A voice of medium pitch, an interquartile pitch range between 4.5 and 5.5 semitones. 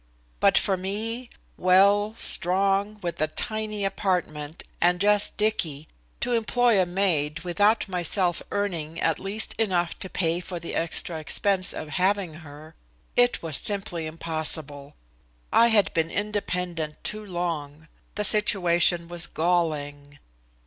No: medium, 180 Hz; average, 3.9 semitones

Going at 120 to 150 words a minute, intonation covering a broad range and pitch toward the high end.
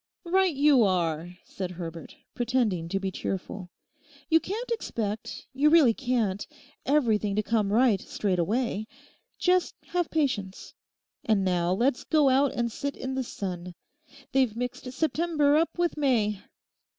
Yes: average, 140 wpm; wide, 6.7 semitones; high, 235 Hz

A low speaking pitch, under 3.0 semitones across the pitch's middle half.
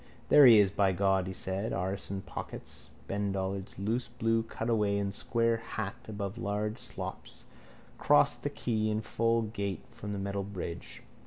Yes: low, 100 Hz; narrow, 2.6 semitones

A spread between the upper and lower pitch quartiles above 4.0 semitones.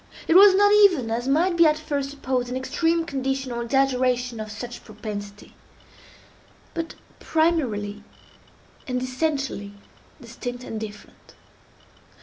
Yes: average, 5.0 semitones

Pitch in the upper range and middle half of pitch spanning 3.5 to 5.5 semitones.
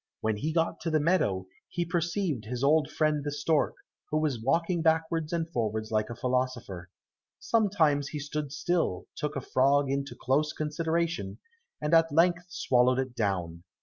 No: medium, 150 Hz; average, 4.5 semitones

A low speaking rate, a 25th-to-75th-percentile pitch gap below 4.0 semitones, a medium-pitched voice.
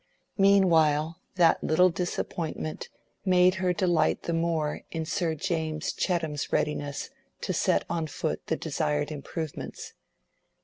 Yes: slow, 120 wpm; narrow, 2.6 semitones; medium, 165 Hz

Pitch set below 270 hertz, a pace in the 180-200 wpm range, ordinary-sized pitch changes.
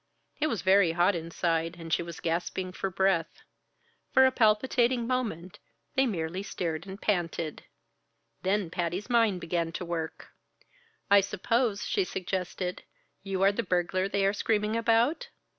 No: high, 190 Hz; average, 145 wpm; average, 4.2 semitones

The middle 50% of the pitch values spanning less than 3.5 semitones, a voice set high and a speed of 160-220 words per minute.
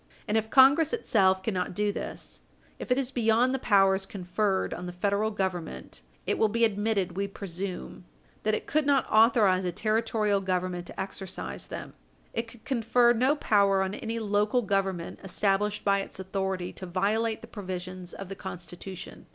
Yes: average, 2.9 semitones; high, 200 Hz; average, 170 wpm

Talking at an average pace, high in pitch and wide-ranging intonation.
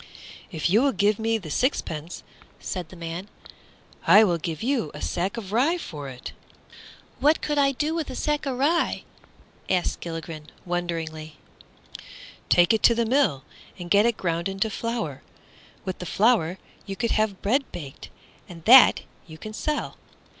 Yes: average, 165 wpm; high, 195 Hz; wide, 6.3 semitones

